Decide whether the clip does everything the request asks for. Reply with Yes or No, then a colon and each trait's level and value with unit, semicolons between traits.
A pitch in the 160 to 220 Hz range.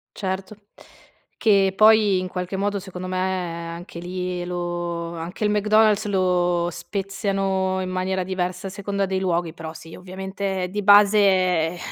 Yes: medium, 185 Hz